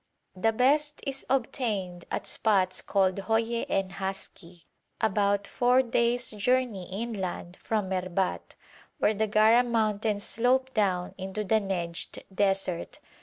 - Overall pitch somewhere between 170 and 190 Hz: No, high, 210 Hz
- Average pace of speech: No, slow, 125 wpm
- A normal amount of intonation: Yes, average, 3.6 semitones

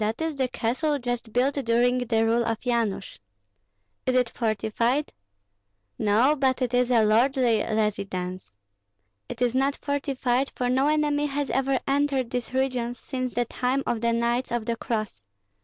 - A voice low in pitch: No, high, 245 Hz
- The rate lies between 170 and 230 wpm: No, average, 160 wpm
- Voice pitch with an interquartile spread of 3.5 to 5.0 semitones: No, average, 2.7 semitones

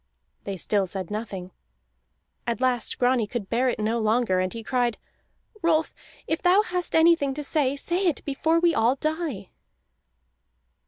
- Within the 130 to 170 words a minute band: Yes, average, 155 wpm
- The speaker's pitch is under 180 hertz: No, very high, 255 Hz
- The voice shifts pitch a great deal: Yes, wide, 6.7 semitones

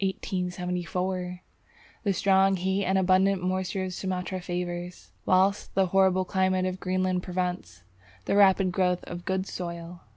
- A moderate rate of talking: No, slow, 130 wpm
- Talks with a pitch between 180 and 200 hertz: Yes, medium, 185 Hz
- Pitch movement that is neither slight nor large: No, narrow, 1.1 semitones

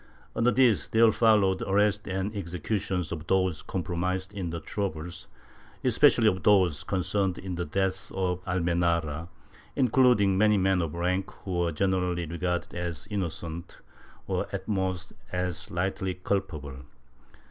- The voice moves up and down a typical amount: No, narrow, 2.2 semitones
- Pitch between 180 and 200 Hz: No, very low, 95 Hz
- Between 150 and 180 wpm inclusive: No, slow, 135 wpm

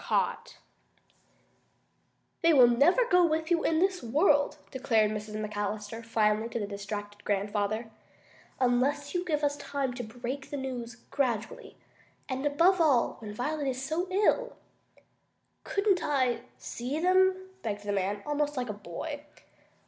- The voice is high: Yes, very high, 260 Hz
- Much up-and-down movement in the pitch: Yes, wide, 6.3 semitones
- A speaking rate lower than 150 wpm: Yes, average, 140 wpm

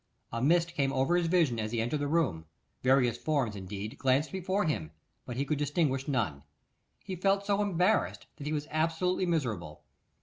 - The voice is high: No, medium, 145 Hz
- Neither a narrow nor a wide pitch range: No, wide, 6.2 semitones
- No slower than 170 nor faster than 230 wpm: Yes, average, 180 wpm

